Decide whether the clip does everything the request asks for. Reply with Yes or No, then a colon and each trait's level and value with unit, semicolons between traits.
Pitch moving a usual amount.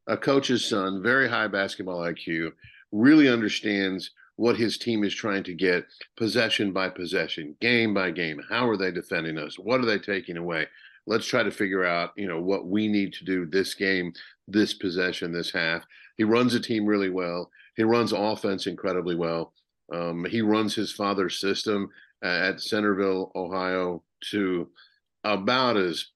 Yes: average, 3.5 semitones